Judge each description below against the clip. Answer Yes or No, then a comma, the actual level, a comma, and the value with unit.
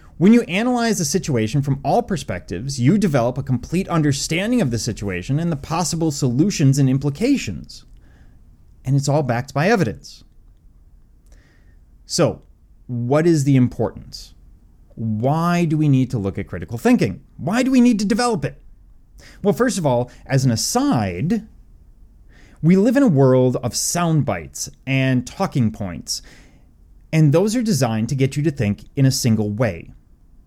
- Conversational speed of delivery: Yes, average, 160 wpm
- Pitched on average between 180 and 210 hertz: No, low, 135 Hz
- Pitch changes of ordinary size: No, wide, 7.8 semitones